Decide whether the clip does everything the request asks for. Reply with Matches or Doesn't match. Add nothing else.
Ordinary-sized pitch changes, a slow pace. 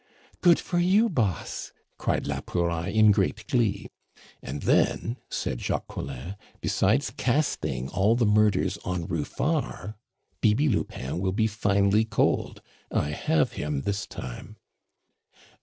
Matches